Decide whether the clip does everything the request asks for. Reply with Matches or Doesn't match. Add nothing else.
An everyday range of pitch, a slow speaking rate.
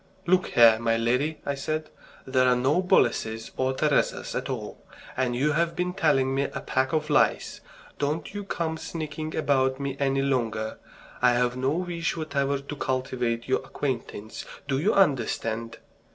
Doesn't match